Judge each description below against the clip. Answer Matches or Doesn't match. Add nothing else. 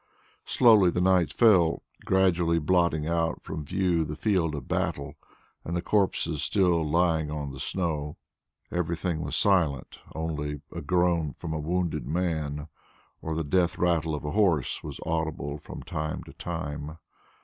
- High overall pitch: Doesn't match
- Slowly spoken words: Doesn't match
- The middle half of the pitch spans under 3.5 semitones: Matches